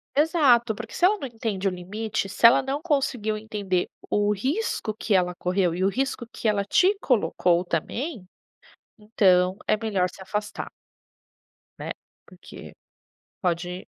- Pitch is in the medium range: No, high, 210 Hz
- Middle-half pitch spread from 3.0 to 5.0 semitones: Yes, average, 4.7 semitones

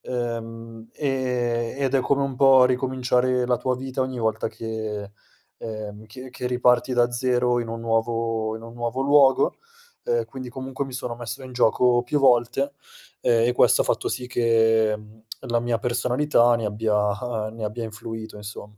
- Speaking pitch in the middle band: No, low, 120 Hz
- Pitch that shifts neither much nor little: No, narrow, 2.2 semitones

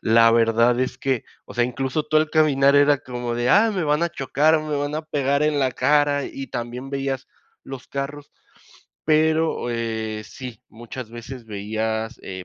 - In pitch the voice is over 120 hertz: Yes, low, 135 Hz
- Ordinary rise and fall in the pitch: Yes, average, 3.8 semitones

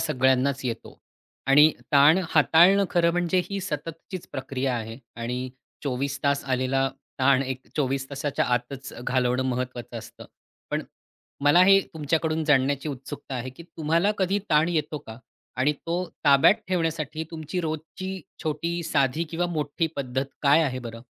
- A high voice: No, medium, 145 Hz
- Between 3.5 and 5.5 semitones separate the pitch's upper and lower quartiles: Yes, average, 3.8 semitones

